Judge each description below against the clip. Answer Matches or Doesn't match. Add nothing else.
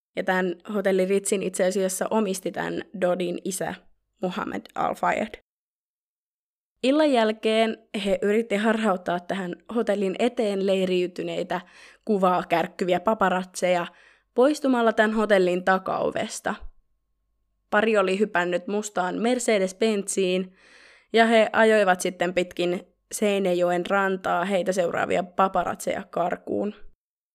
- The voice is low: Doesn't match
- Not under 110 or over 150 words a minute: Doesn't match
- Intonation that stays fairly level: Doesn't match